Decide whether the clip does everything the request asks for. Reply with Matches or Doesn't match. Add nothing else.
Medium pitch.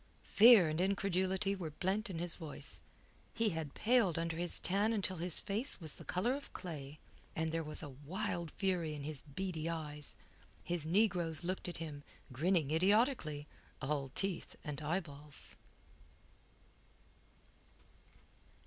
Matches